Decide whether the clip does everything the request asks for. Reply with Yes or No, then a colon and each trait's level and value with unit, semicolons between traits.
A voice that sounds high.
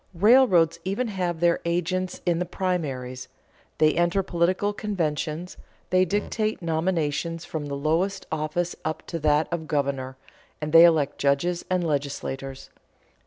No: medium, 170 Hz